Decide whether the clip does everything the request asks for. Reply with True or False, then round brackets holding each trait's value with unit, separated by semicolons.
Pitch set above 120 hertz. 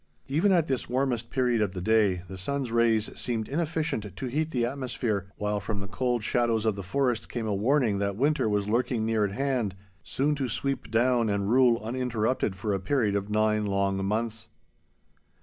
False (115 Hz)